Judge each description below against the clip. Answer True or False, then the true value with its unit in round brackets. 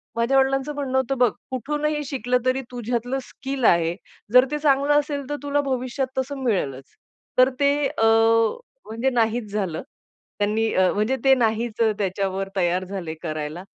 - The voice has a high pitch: True (245 Hz)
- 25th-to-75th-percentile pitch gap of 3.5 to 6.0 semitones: True (4.8 semitones)